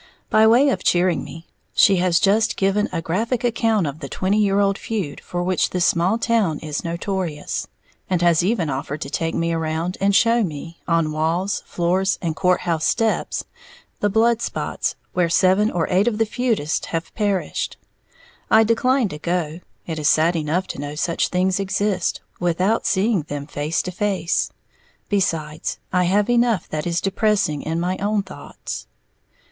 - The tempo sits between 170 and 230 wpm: Yes, average, 175 wpm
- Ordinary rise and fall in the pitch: Yes, average, 4.0 semitones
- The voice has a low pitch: No, medium, 180 Hz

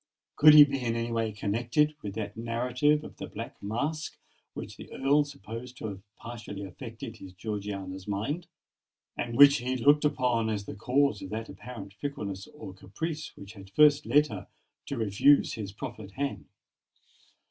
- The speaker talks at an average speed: Yes, average, 170 wpm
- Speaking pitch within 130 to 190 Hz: No, low, 115 Hz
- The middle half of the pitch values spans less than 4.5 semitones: No, wide, 5.6 semitones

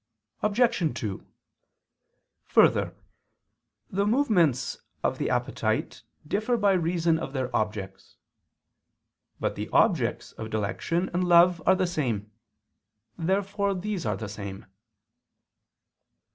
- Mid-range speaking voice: Yes, medium, 170 Hz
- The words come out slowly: Yes, slow, 105 wpm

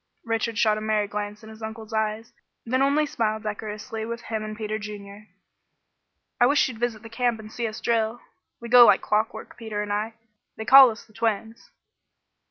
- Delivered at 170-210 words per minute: Yes, average, 190 wpm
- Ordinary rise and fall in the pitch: No, narrow, 1.4 semitones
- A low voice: No, high, 220 Hz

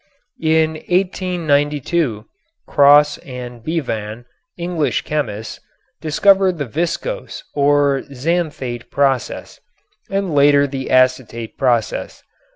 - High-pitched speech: No, medium, 145 Hz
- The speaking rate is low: Yes, slow, 85 wpm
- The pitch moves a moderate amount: Yes, average, 4.5 semitones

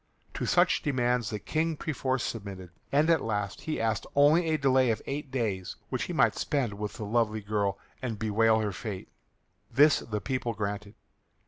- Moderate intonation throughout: Yes, average, 4.8 semitones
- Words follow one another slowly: No, average, 180 wpm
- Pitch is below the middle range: Yes, low, 115 Hz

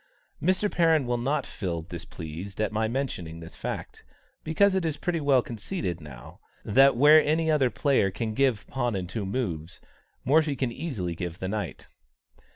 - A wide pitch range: Yes, wide, 8.2 semitones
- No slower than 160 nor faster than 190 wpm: Yes, average, 170 wpm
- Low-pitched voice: Yes, low, 120 Hz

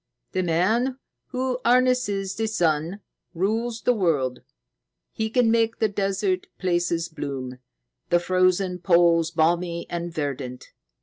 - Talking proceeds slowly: Yes, slow, 120 wpm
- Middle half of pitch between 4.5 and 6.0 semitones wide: Yes, average, 4.8 semitones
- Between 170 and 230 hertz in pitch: Yes, medium, 185 Hz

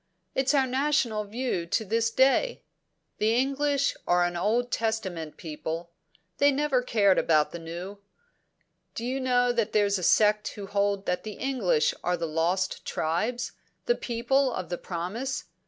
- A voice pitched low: No, high, 215 Hz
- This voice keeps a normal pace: Yes, average, 155 wpm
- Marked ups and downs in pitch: Yes, wide, 6.3 semitones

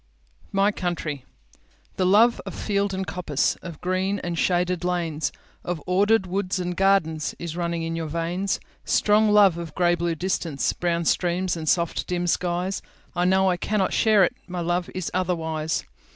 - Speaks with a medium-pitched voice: Yes, medium, 180 Hz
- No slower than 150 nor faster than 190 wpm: No, average, 140 wpm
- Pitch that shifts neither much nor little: No, narrow, 2.1 semitones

